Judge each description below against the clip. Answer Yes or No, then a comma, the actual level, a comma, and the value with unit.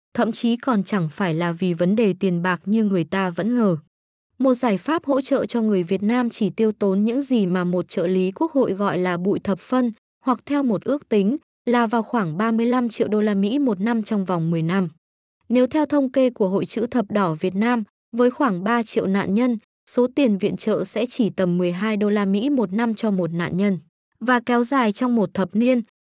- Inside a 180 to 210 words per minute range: No, average, 235 wpm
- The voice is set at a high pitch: Yes, high, 215 Hz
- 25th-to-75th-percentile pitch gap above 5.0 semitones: No, average, 4.1 semitones